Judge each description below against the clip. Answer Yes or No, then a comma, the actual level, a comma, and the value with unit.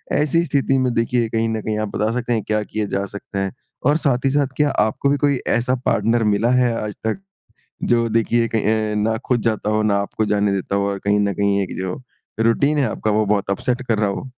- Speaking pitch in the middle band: No, low, 110 Hz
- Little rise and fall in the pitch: No, average, 3.1 semitones